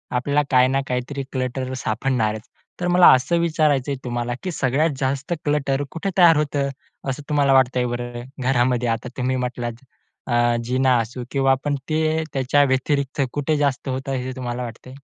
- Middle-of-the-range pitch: No, low, 130 Hz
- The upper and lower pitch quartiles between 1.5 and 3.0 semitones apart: Yes, narrow, 2.6 semitones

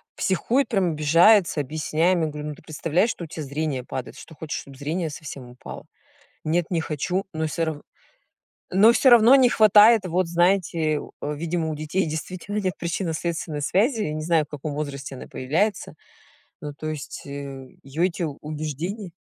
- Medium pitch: Yes, medium, 160 Hz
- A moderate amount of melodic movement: Yes, average, 3.7 semitones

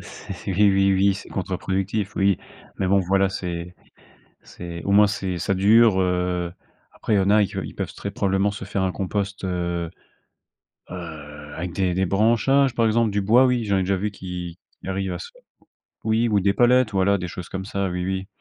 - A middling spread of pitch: No, narrow, 2.2 semitones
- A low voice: Yes, very low, 95 Hz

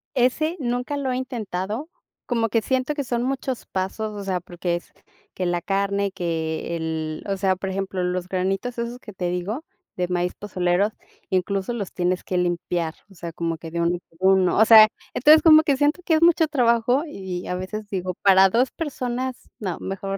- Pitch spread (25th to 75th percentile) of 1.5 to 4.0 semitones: No, wide, 5.4 semitones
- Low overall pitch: No, high, 195 Hz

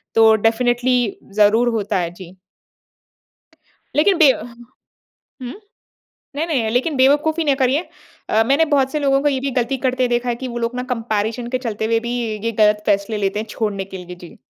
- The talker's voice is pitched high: Yes, high, 235 Hz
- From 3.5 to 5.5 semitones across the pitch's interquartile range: Yes, average, 3.8 semitones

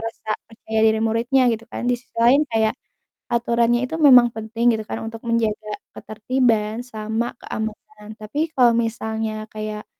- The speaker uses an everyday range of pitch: No, narrow, 1.7 semitones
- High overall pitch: Yes, high, 225 Hz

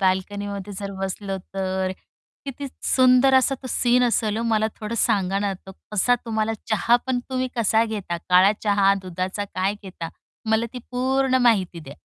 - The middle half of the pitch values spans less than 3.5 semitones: No, average, 4.0 semitones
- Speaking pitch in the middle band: No, high, 205 Hz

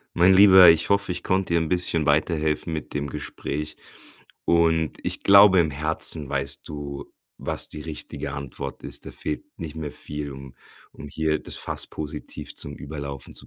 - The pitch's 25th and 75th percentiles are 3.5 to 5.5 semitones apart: No, average, 2.7 semitones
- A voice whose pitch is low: Yes, very low, 75 Hz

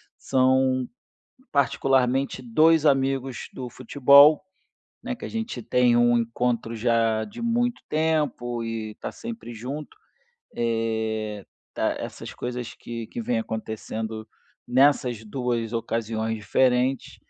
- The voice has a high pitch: No, low, 125 Hz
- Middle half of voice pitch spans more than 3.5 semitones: No, average, 3.1 semitones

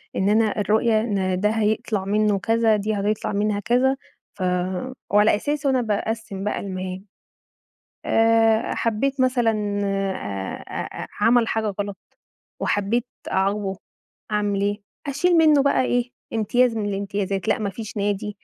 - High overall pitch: Yes, high, 210 Hz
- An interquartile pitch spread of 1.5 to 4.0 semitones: Yes, narrow, 2.4 semitones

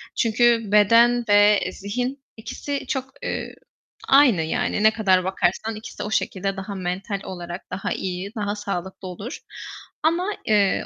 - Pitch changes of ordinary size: Yes, average, 3.7 semitones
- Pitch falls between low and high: No, high, 205 Hz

